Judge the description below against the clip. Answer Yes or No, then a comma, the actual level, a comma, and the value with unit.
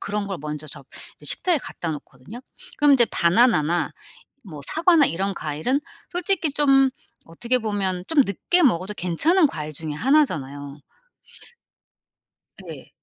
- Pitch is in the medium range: No, high, 200 Hz